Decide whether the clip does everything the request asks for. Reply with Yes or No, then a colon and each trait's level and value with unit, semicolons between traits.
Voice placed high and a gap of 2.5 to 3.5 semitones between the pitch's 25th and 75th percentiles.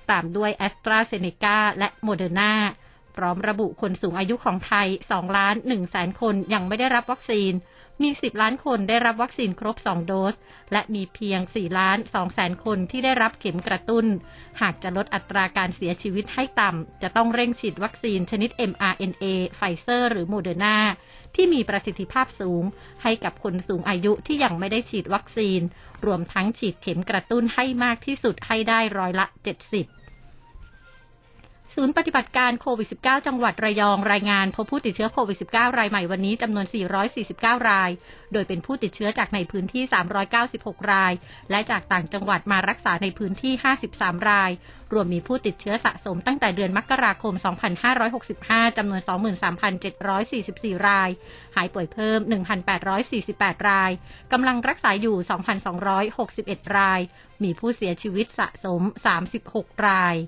Yes: high, 205 Hz; average, 3.1 semitones